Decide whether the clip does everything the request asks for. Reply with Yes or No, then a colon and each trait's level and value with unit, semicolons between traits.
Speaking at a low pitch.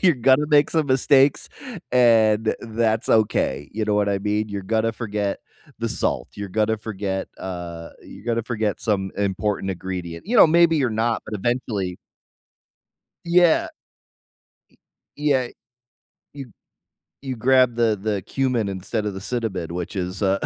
Yes: low, 110 Hz